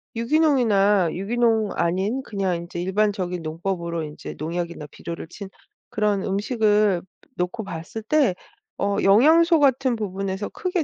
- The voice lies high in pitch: Yes, high, 200 Hz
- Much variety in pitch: No, average, 4.5 semitones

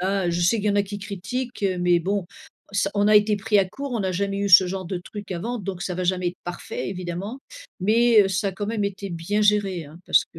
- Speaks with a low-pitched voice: No, high, 195 Hz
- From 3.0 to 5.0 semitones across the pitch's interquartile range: No, narrow, 2.4 semitones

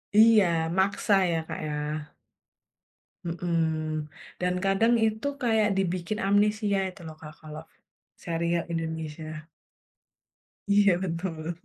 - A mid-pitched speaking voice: Yes, medium, 175 Hz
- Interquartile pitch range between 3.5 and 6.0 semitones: Yes, average, 4.0 semitones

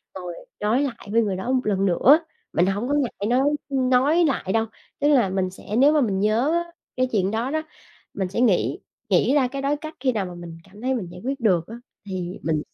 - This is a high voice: Yes, high, 225 Hz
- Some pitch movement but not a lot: No, wide, 5.8 semitones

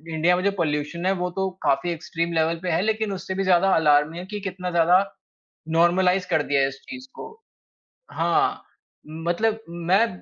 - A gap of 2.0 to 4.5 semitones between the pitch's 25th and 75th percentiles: Yes, narrow, 2.6 semitones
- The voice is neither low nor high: Yes, medium, 175 Hz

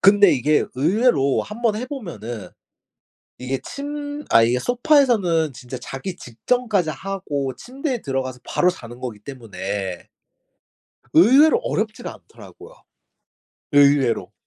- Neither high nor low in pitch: Yes, medium, 155 Hz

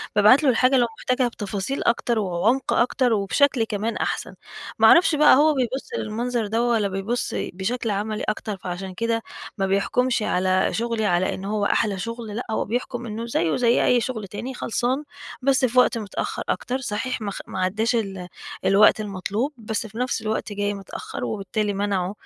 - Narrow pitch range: No, average, 3.6 semitones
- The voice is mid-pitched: No, high, 220 Hz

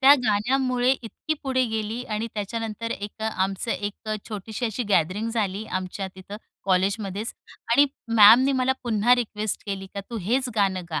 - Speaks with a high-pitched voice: Yes, high, 215 Hz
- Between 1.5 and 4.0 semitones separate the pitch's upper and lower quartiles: Yes, average, 3.3 semitones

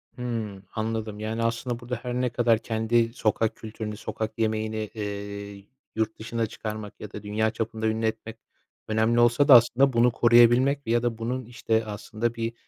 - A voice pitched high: No, low, 115 Hz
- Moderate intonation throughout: No, narrow, 1.5 semitones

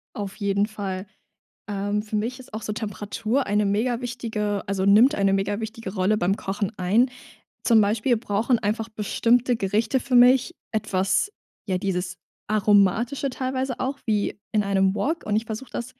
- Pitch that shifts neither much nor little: Yes, average, 3.0 semitones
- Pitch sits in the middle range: No, high, 215 Hz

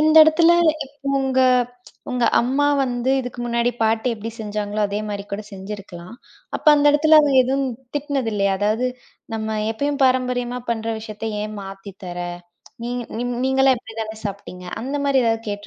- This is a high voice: Yes, high, 235 Hz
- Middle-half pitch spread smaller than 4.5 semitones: Yes, average, 4.0 semitones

